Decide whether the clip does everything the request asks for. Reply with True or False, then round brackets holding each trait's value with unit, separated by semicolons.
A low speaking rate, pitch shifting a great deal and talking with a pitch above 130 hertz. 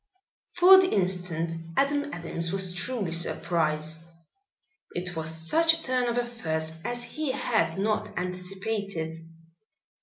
True (120 wpm; 6.8 semitones; 185 Hz)